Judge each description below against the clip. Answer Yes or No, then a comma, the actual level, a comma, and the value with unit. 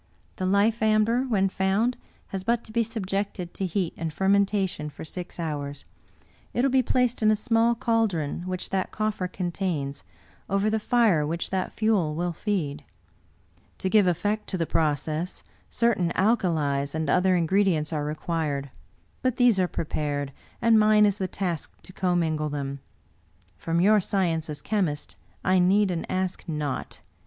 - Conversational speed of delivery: Yes, average, 160 wpm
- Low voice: No, medium, 185 Hz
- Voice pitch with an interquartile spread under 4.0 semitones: No, average, 5.0 semitones